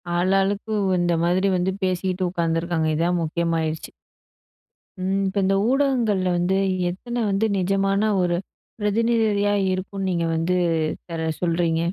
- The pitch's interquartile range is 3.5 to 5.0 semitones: No, narrow, 2.6 semitones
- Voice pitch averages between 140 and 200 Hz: Yes, medium, 185 Hz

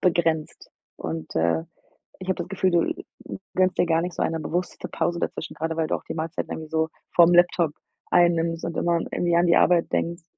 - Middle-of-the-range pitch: Yes, medium, 170 Hz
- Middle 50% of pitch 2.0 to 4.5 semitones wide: No, narrow, 1.3 semitones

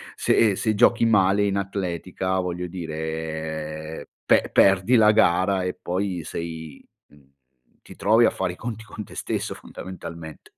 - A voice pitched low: Yes, very low, 90 Hz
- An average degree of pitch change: Yes, average, 3.9 semitones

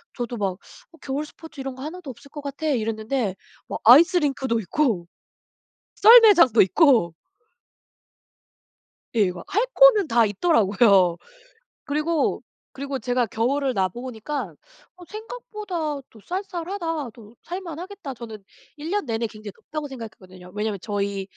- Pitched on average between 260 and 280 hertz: Yes, very high, 265 Hz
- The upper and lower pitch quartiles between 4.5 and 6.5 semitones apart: No, wide, 7.1 semitones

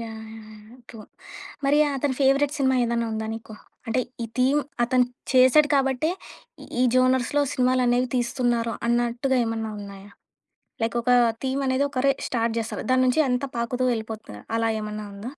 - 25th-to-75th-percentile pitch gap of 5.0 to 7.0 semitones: No, narrow, 2.5 semitones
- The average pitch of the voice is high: Yes, high, 245 Hz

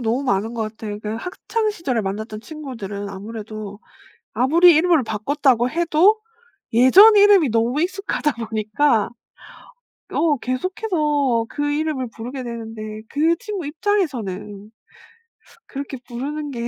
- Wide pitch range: Yes, wide, 6.2 semitones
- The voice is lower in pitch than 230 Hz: No, very high, 260 Hz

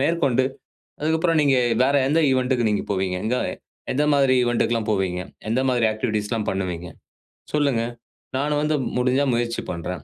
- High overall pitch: No, low, 125 Hz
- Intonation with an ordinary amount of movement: Yes, average, 5.0 semitones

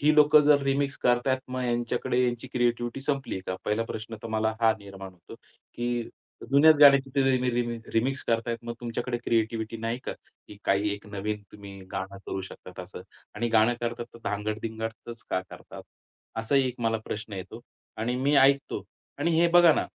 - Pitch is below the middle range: Yes, low, 120 Hz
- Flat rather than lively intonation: No, average, 3.3 semitones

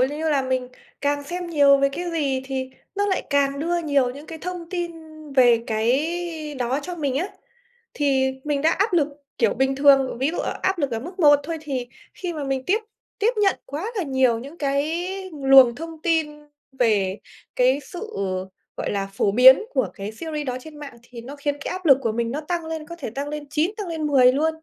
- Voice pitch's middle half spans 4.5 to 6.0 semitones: No, average, 3.9 semitones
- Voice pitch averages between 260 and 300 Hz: Yes, very high, 285 Hz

